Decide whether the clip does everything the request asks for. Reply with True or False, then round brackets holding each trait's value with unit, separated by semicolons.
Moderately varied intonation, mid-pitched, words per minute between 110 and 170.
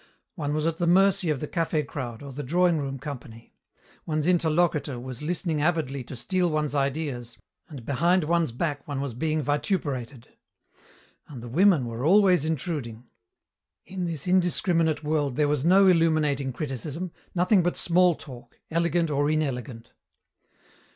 True (4.0 semitones; 150 Hz; 150 wpm)